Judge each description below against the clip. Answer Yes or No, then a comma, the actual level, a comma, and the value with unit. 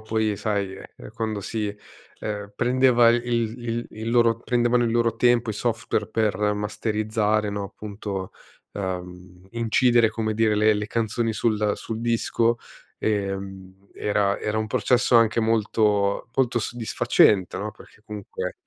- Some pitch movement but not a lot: No, narrow, 2.2 semitones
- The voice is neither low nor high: No, low, 110 Hz